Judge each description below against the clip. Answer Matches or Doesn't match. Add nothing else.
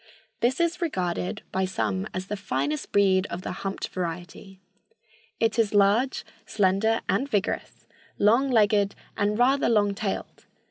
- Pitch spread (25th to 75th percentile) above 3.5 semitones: Doesn't match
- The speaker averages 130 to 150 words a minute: Matches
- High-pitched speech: Matches